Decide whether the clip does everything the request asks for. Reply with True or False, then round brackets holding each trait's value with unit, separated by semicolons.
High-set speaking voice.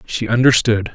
False (115 Hz)